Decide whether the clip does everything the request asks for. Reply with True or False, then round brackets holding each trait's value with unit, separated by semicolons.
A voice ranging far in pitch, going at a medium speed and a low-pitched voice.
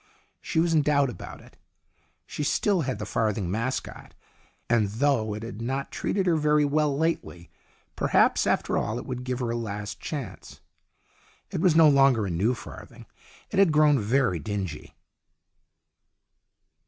True (5.8 semitones; 155 wpm; 130 Hz)